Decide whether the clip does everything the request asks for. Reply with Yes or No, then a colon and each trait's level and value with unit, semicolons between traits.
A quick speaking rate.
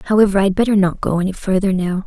Yes: fast, 235 wpm